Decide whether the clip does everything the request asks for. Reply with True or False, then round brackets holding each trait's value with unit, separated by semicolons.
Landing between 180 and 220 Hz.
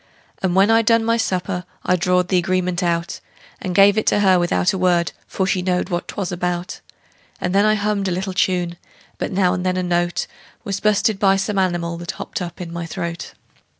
True (185 Hz)